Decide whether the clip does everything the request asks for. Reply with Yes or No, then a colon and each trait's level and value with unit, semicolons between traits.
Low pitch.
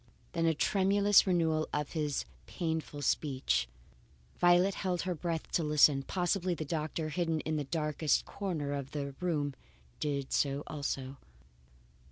No: medium, 155 Hz